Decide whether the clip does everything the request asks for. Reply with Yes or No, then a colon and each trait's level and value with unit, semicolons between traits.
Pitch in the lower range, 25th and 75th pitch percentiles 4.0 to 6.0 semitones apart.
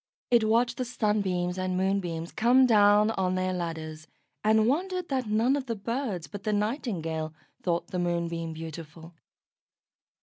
No: high, 195 Hz; average, 5.2 semitones